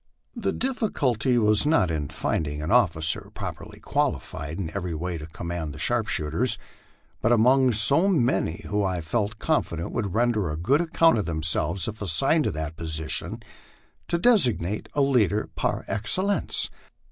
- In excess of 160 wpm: No, average, 155 wpm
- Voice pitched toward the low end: Yes, low, 105 Hz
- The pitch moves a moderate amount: No, wide, 7.7 semitones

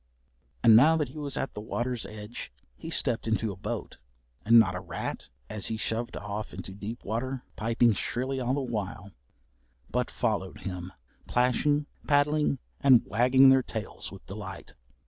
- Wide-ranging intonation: No, average, 3.9 semitones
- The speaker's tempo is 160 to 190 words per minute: Yes, average, 165 wpm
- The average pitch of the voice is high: No, low, 115 Hz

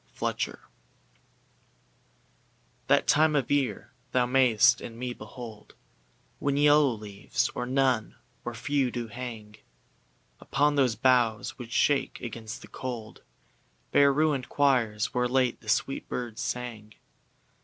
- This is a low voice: Yes, low, 125 Hz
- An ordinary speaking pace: No, slow, 120 wpm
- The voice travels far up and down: No, average, 3.2 semitones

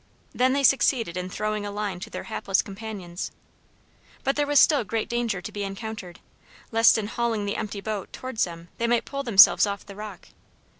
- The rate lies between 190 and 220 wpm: Yes, average, 195 wpm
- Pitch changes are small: No, average, 3.2 semitones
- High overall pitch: Yes, high, 215 Hz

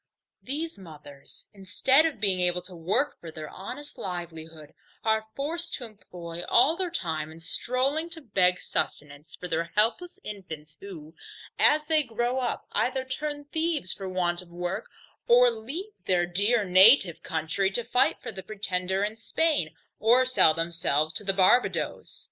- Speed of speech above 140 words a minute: Yes, average, 160 wpm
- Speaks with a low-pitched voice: No, high, 195 Hz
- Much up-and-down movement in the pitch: Yes, wide, 6.8 semitones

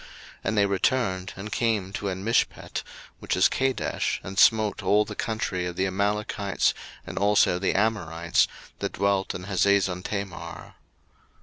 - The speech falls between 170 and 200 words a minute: No, average, 140 wpm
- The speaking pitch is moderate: No, low, 100 Hz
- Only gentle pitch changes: Yes, narrow, 2.2 semitones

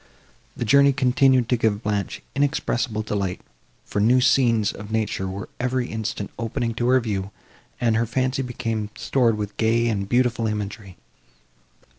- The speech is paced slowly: No, average, 150 wpm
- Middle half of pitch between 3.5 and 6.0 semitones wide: No, average, 3.1 semitones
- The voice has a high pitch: No, low, 115 Hz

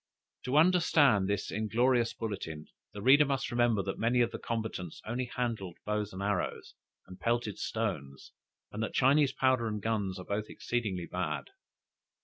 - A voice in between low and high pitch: No, low, 110 Hz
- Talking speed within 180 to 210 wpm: No, average, 155 wpm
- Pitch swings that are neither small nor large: Yes, average, 3.8 semitones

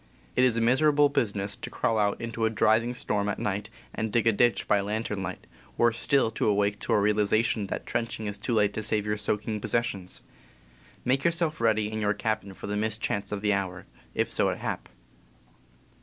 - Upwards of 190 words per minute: Yes, average, 200 wpm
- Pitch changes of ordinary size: No, narrow, 2.1 semitones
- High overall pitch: No, low, 110 Hz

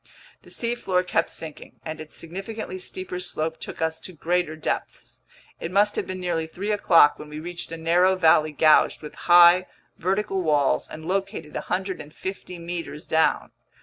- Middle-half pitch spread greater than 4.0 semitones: No, average, 2.8 semitones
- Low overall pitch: No, medium, 175 Hz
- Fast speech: No, average, 160 wpm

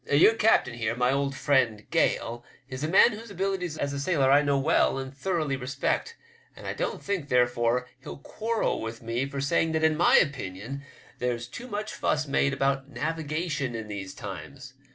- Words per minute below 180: No, average, 185 wpm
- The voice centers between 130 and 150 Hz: Yes, medium, 140 Hz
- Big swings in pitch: No, average, 4.6 semitones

